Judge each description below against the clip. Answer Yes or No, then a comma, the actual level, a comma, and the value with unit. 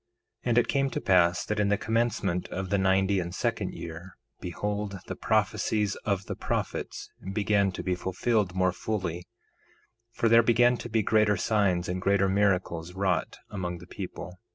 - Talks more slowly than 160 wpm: No, average, 175 wpm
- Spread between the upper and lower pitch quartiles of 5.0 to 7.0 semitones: No, average, 2.9 semitones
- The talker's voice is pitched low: Yes, low, 100 Hz